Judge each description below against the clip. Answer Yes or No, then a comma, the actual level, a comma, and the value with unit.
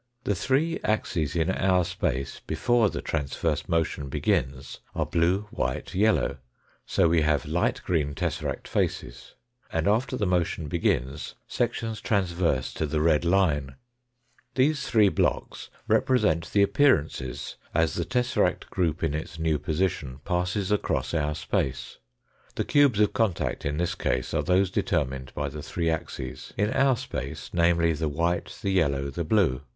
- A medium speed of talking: Yes, average, 150 wpm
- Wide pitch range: No, average, 5.0 semitones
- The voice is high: No, very low, 85 Hz